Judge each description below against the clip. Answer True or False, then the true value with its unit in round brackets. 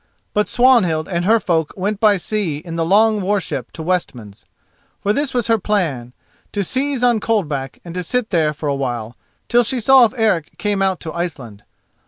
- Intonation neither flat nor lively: False (5.8 semitones)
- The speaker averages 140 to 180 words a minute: False (200 wpm)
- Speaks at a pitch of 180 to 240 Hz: True (190 Hz)